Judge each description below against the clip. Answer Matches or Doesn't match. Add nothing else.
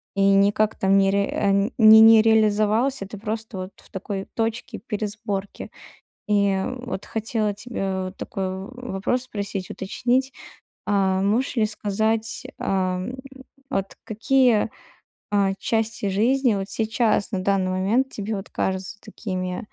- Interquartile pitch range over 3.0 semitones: Doesn't match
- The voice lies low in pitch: Doesn't match